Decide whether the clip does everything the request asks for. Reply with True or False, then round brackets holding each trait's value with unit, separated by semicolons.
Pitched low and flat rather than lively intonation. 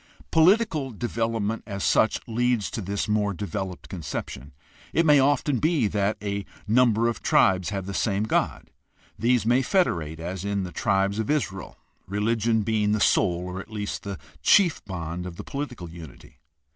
False (105 Hz; 3.9 semitones)